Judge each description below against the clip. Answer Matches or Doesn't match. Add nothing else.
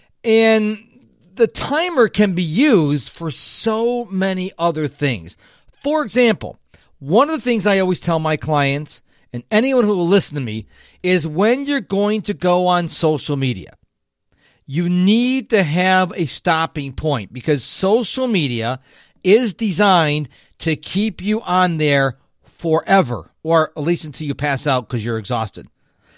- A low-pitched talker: Doesn't match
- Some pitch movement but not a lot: Doesn't match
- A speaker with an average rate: Matches